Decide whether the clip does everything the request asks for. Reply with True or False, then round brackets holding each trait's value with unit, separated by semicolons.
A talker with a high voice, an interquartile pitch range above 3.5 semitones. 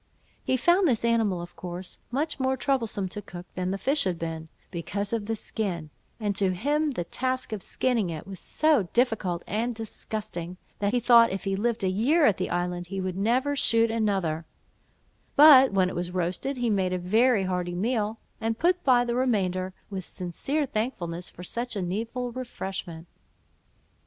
True (210 Hz; 5.1 semitones)